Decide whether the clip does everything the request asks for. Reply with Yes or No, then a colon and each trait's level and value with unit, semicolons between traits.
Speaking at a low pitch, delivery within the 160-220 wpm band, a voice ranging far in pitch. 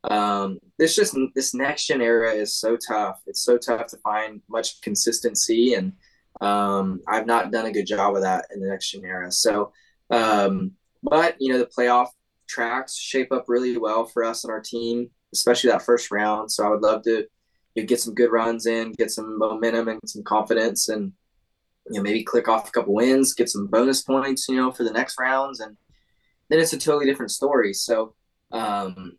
No: low, 115 Hz; fast, 205 wpm; average, 2.8 semitones